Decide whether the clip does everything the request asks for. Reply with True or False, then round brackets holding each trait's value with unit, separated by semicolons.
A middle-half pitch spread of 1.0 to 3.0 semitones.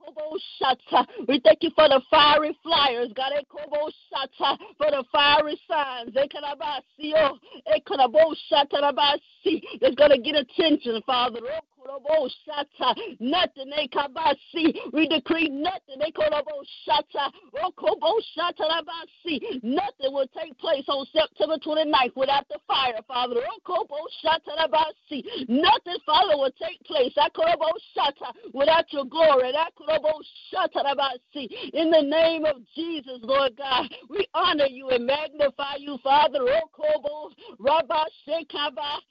True (2.6 semitones)